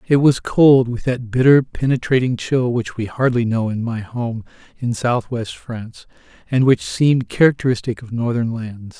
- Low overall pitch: Yes, low, 120 Hz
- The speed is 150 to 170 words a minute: Yes, average, 165 wpm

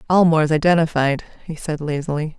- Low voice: No, medium, 155 Hz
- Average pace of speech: No, slow, 125 wpm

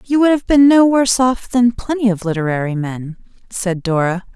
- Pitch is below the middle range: No, high, 220 Hz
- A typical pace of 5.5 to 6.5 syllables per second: No, 5.1 syllables/s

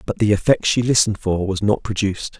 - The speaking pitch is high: No, low, 105 Hz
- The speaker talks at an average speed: No, fast, 225 wpm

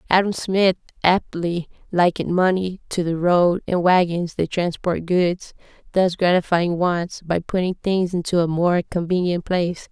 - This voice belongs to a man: No, female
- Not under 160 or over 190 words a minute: No, average, 145 wpm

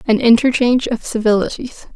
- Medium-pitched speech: No, high, 235 Hz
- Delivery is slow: Yes, slow, 125 wpm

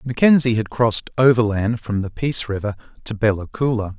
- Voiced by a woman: No, male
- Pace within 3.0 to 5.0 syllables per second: No, 5.7 syllables/s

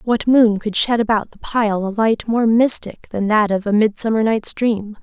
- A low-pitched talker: No, high, 220 Hz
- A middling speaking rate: No, fast, 215 wpm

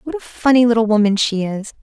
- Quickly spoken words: Yes, fast, 230 wpm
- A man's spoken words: No, female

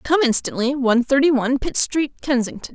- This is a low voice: No, very high, 270 Hz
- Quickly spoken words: No, average, 175 wpm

